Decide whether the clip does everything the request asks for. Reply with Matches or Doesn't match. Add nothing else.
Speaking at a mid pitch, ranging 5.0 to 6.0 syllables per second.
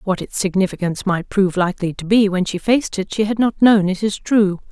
Doesn't match